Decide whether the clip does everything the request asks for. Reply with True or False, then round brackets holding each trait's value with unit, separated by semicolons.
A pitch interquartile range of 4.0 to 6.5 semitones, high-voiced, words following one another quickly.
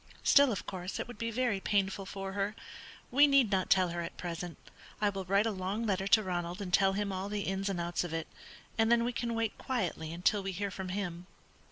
False (2.7 semitones; 195 Hz; 235 wpm)